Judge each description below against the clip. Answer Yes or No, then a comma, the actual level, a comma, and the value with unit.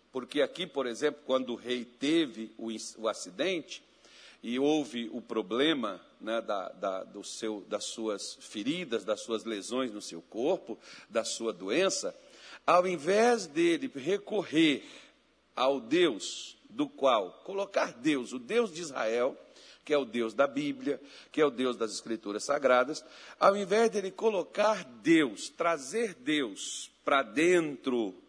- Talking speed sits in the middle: Yes, average, 140 wpm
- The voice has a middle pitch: Yes, medium, 155 Hz